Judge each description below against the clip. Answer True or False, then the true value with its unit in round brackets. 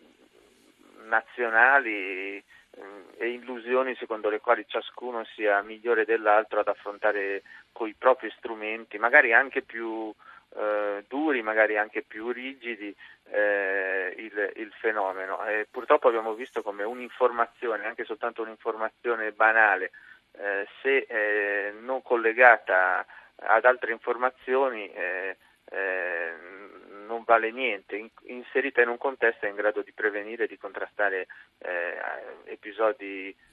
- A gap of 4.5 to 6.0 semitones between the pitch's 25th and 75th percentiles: False (3.0 semitones)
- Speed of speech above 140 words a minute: False (120 wpm)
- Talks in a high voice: False (115 Hz)